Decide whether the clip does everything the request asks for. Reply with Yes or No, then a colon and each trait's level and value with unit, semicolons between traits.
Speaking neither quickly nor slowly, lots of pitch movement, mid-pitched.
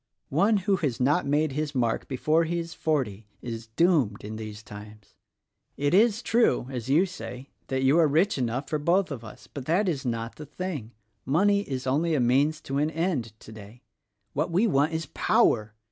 Yes: average, 195 wpm; wide, 6.0 semitones; medium, 145 Hz